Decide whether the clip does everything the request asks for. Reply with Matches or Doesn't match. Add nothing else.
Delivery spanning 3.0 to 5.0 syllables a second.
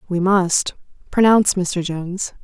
Matches